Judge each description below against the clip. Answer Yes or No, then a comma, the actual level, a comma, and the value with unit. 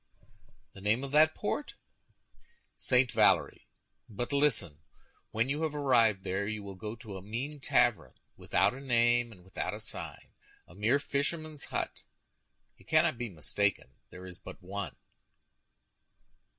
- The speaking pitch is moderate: No, low, 115 Hz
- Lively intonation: Yes, wide, 5.9 semitones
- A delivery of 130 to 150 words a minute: Yes, average, 140 wpm